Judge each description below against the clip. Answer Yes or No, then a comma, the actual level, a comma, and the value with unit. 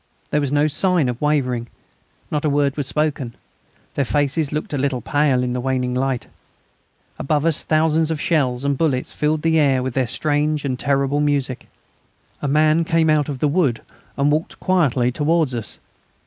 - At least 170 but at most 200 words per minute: Yes, average, 180 wpm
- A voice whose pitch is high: No, medium, 145 Hz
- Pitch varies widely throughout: No, average, 2.8 semitones